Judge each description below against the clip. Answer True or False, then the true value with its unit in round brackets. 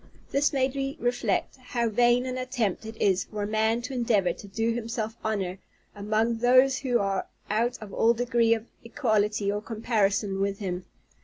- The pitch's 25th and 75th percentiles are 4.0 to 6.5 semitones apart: False (2.9 semitones)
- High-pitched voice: True (225 Hz)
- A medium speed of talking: True (175 wpm)